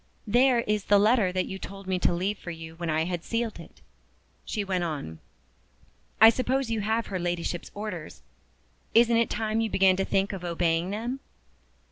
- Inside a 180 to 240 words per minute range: Yes, average, 185 wpm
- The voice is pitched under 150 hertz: No, high, 195 Hz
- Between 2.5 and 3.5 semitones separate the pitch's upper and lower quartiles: No, average, 4.2 semitones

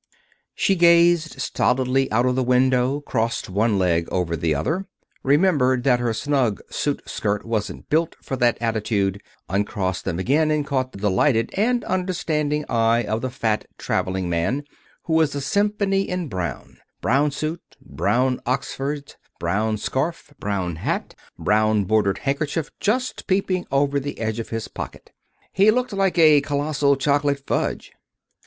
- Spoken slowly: No, average, 150 wpm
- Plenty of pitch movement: Yes, wide, 6.0 semitones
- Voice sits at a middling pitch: No, low, 130 Hz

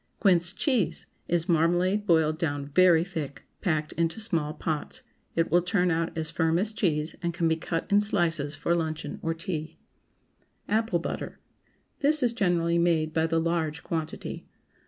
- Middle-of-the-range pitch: Yes, medium, 165 Hz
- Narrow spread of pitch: Yes, narrow, 2.1 semitones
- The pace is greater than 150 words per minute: Yes, average, 160 wpm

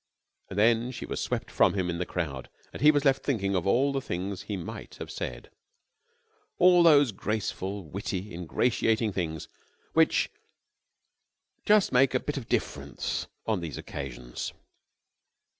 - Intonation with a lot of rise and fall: Yes, wide, 6.8 semitones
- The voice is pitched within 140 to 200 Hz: No, low, 105 Hz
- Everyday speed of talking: Yes, average, 150 wpm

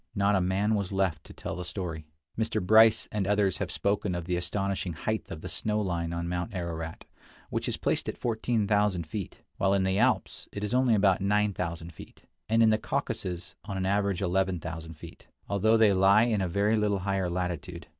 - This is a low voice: Yes, very low, 95 Hz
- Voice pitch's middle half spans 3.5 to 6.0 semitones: No, average, 2.9 semitones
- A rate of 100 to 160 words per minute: No, average, 200 wpm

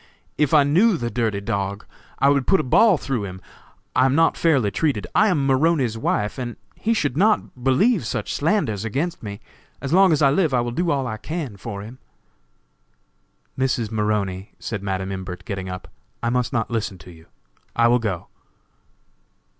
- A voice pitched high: No, low, 125 Hz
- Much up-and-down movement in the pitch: Yes, wide, 6.5 semitones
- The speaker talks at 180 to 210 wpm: Yes, average, 185 wpm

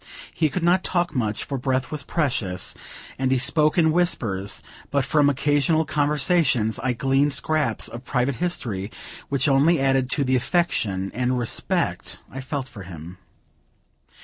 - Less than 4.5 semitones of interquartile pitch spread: Yes, average, 3.7 semitones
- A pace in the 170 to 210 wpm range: No, average, 150 wpm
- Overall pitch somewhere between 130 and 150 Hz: Yes, low, 135 Hz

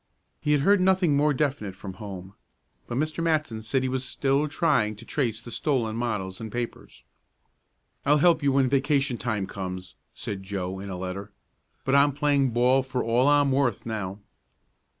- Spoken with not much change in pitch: No, wide, 5.4 semitones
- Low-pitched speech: Yes, low, 125 Hz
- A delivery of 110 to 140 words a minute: No, average, 175 wpm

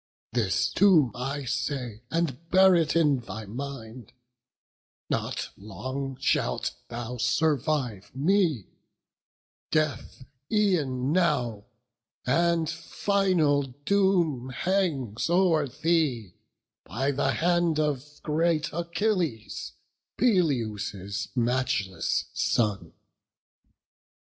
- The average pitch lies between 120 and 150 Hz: Yes, medium, 140 Hz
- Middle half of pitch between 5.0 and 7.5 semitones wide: Yes, wide, 5.6 semitones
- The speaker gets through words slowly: Yes, slow, 85 wpm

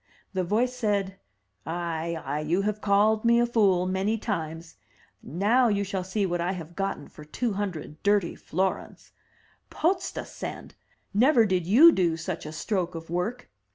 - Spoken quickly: No, average, 155 wpm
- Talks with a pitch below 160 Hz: No, high, 190 Hz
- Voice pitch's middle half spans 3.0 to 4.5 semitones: Yes, average, 4.1 semitones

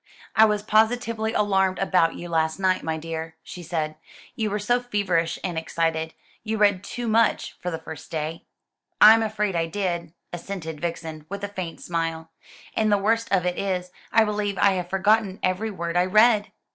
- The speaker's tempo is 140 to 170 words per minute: No, average, 185 wpm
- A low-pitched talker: No, medium, 185 Hz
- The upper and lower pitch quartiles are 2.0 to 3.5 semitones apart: No, average, 4.2 semitones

